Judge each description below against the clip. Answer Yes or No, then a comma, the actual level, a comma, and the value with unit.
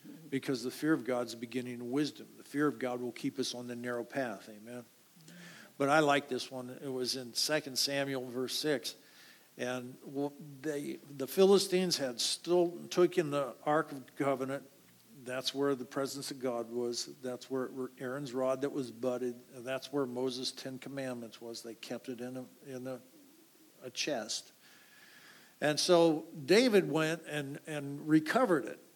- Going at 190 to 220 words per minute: No, average, 175 wpm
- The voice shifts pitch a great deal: No, average, 3.1 semitones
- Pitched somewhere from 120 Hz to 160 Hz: Yes, low, 135 Hz